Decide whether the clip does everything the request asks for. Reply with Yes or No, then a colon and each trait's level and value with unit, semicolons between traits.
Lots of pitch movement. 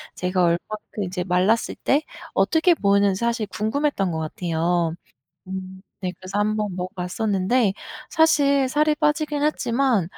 Yes: wide, 7.1 semitones